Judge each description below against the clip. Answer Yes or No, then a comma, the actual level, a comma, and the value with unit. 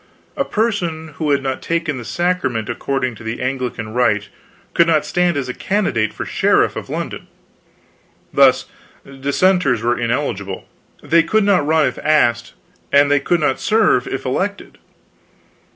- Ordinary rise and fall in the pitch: No, wide, 5.9 semitones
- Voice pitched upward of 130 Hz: Yes, medium, 140 Hz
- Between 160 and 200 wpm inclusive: No, average, 150 wpm